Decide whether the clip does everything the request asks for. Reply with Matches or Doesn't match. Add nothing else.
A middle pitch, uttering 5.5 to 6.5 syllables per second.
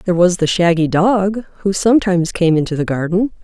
Matches